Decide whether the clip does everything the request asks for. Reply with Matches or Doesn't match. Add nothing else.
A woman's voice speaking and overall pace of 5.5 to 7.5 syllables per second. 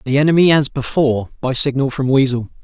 Doesn't match